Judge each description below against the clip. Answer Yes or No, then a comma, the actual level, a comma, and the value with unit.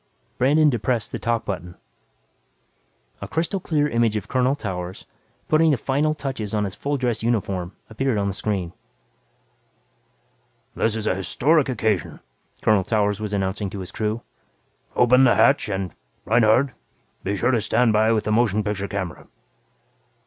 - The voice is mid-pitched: No, low, 110 Hz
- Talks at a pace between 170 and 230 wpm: No, average, 155 wpm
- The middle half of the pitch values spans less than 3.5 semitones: No, average, 4.3 semitones